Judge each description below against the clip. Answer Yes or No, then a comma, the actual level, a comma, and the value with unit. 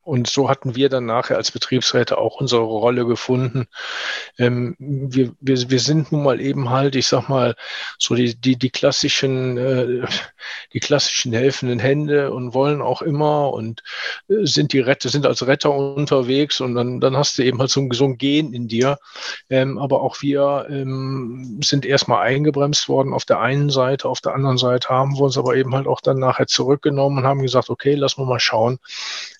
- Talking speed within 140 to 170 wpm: No, fast, 190 wpm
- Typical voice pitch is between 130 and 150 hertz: Yes, low, 135 Hz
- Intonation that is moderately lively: No, narrow, 1.8 semitones